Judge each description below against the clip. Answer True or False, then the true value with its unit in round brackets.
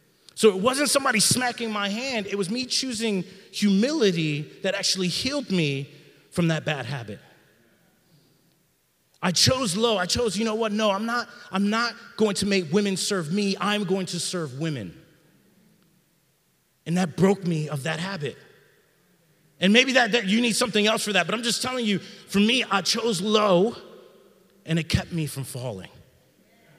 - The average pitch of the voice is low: False (195 Hz)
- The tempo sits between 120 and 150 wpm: False (170 wpm)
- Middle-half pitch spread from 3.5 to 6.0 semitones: True (4.7 semitones)